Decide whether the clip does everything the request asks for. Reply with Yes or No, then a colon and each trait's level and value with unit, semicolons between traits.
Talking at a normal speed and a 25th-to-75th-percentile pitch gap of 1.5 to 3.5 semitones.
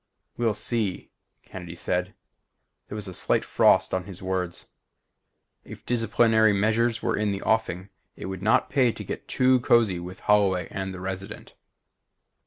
Yes: average, 155 wpm; average, 3.2 semitones